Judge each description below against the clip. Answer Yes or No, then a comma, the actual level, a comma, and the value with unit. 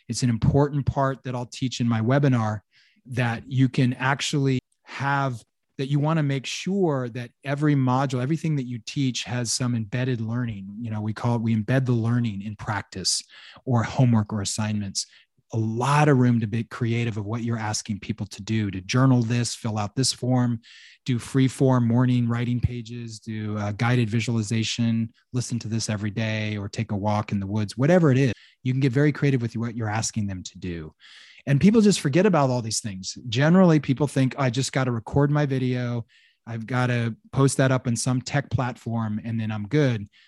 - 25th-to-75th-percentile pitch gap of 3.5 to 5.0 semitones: No, average, 3.0 semitones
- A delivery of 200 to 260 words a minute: Yes, fast, 205 wpm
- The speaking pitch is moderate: No, low, 120 Hz